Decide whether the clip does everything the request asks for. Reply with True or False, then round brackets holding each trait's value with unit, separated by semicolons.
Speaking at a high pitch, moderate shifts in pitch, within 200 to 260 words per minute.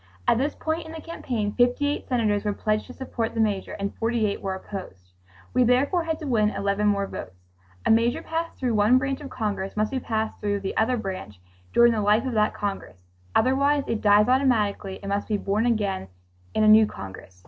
True (220 Hz; 3.9 semitones; 205 wpm)